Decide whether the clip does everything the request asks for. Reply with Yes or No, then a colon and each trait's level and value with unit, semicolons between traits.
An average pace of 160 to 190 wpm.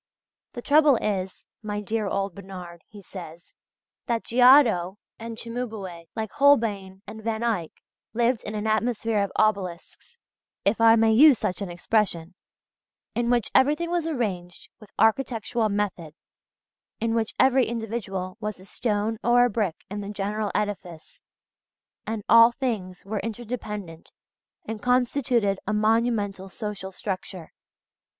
No: slow, 135 wpm